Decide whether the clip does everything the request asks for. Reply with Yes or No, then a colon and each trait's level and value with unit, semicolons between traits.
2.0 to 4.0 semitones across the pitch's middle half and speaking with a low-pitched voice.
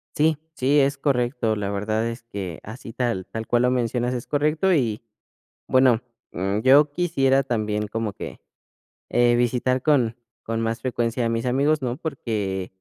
Yes: average, 3.2 semitones; low, 120 Hz